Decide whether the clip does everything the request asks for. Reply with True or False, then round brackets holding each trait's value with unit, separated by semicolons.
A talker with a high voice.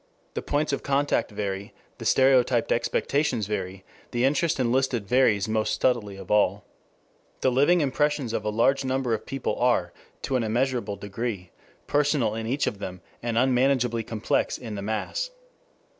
False (120 Hz)